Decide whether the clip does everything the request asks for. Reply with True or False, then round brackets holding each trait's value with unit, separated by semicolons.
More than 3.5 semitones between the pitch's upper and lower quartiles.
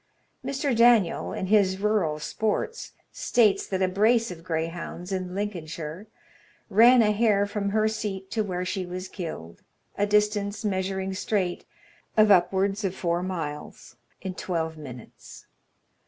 False (2.9 semitones)